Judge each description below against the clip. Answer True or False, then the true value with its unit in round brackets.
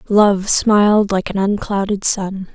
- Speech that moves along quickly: False (140 wpm)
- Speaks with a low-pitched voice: False (200 Hz)